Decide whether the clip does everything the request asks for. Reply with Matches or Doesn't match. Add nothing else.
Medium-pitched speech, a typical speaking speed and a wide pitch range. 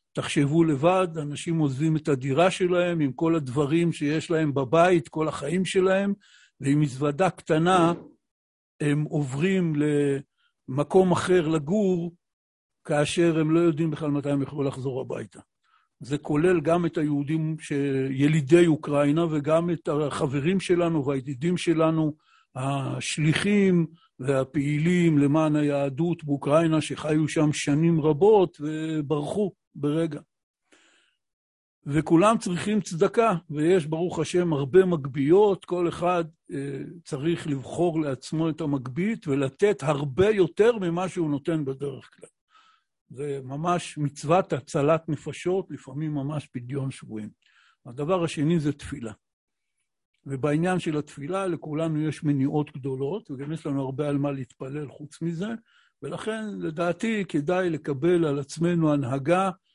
Doesn't match